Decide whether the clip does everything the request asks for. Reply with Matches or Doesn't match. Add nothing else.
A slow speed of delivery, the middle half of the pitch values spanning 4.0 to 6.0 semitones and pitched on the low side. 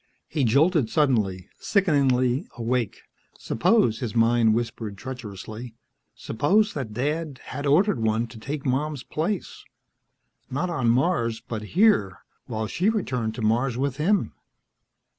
Matches